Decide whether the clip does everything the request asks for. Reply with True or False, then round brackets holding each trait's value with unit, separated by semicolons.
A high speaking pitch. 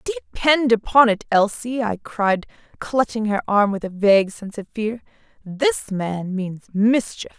True (220 Hz)